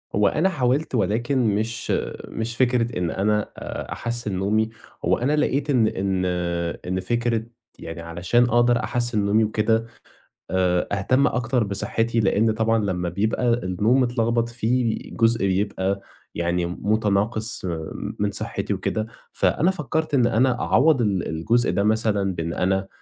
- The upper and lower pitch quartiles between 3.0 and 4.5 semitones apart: Yes, average, 3.5 semitones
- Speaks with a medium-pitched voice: No, low, 110 Hz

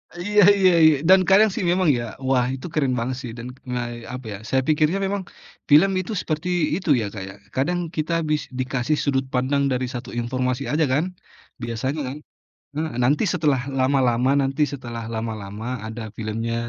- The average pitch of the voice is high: No, low, 130 Hz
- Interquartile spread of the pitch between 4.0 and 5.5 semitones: Yes, average, 4.5 semitones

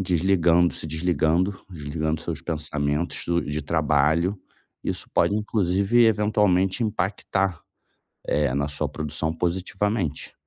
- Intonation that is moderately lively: Yes, average, 3.9 semitones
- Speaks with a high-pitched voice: No, very low, 85 Hz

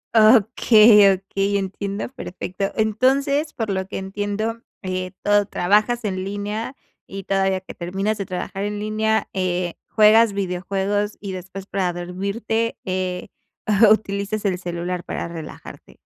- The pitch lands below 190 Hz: No, high, 200 Hz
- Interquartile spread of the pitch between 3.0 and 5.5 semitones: No, narrow, 2.5 semitones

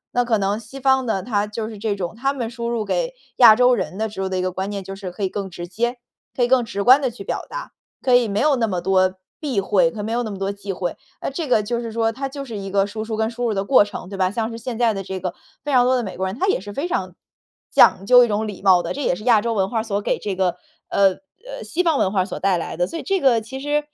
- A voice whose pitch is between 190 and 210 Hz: No, high, 220 Hz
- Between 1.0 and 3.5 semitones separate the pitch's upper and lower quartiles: No, average, 4.1 semitones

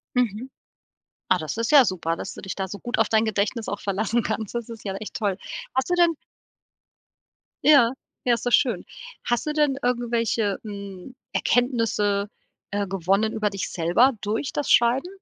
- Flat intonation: No, average, 3.4 semitones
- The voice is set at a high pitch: Yes, high, 220 Hz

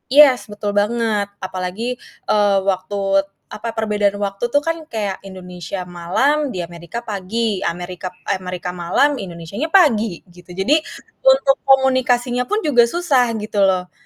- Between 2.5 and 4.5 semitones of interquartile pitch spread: No, average, 5.1 semitones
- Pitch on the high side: Yes, high, 210 Hz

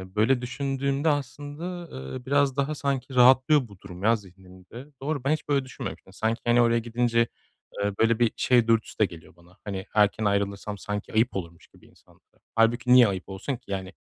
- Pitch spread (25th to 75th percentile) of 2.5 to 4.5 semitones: No, average, 5.0 semitones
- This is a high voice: No, low, 115 Hz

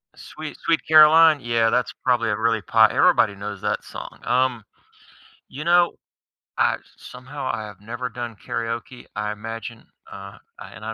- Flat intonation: No, average, 3.0 semitones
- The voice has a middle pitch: No, low, 115 Hz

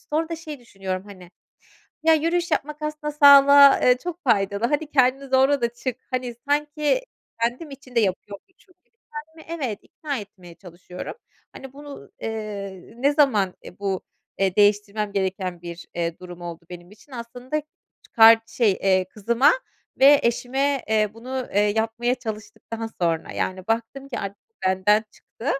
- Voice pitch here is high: Yes, high, 235 Hz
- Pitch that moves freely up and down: Yes, wide, 6.0 semitones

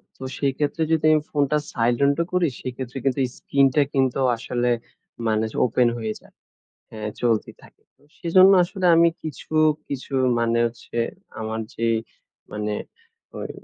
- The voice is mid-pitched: No, low, 130 Hz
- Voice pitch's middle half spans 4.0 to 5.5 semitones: Yes, average, 4.3 semitones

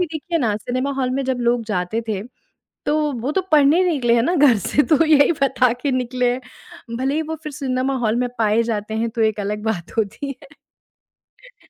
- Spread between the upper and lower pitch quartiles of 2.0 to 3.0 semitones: No, average, 4.2 semitones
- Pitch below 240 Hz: No, very high, 255 Hz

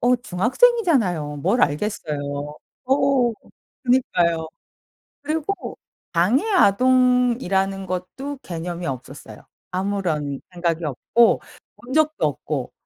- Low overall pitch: No, high, 195 Hz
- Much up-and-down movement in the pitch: Yes, wide, 7.9 semitones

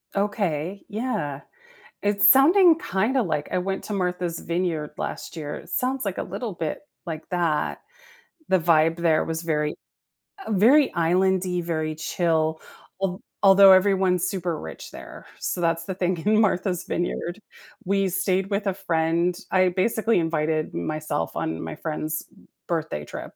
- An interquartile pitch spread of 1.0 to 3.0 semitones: No, average, 3.4 semitones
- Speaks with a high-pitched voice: No, medium, 180 Hz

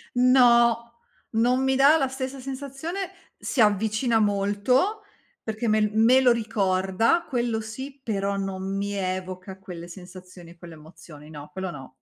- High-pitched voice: Yes, high, 215 Hz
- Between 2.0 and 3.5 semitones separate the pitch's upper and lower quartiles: No, average, 5.2 semitones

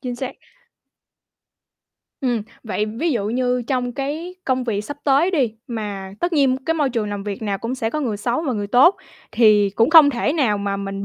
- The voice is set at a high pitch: Yes, high, 245 Hz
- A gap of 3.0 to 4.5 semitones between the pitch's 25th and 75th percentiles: No, average, 4.9 semitones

